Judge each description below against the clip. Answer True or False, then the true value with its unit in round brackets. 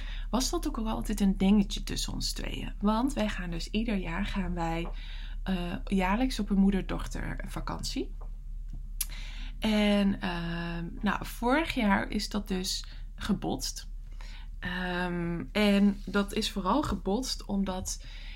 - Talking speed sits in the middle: False (130 wpm)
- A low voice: False (195 Hz)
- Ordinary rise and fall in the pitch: True (3.6 semitones)